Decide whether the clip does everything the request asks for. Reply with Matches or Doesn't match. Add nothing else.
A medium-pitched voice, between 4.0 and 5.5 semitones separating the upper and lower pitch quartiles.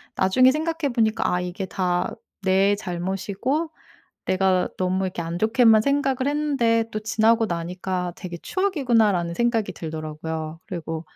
Doesn't match